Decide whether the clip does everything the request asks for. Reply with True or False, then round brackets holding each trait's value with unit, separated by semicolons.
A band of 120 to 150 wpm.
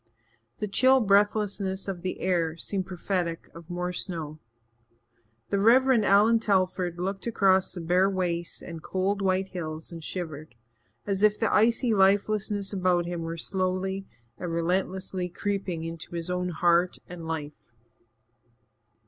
True (140 wpm)